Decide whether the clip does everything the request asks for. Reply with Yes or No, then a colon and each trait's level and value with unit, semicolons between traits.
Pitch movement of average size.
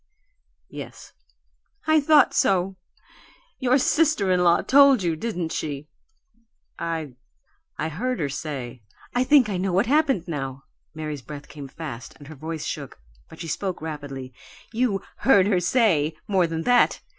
No: wide, 7.5 semitones